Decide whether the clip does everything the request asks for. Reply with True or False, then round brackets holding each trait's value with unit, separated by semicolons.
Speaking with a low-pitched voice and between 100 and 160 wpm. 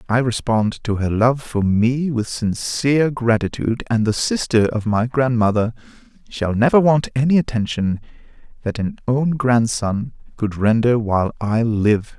True (120 Hz; 150 wpm)